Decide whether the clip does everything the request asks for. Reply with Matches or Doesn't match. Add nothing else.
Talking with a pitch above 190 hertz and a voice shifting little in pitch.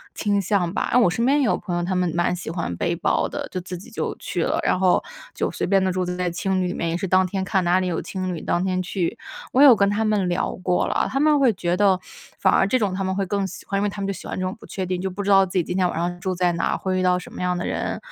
Doesn't match